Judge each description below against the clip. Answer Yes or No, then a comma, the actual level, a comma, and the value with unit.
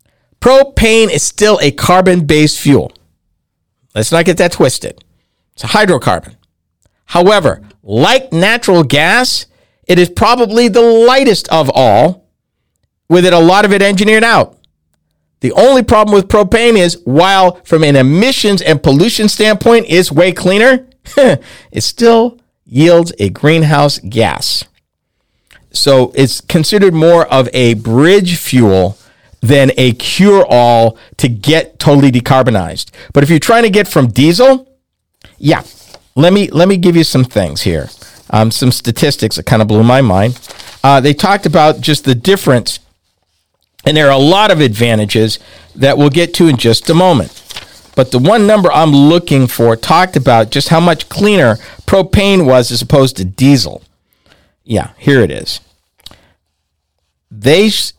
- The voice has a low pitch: No, medium, 145 Hz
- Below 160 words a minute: Yes, average, 150 wpm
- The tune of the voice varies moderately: No, wide, 8.3 semitones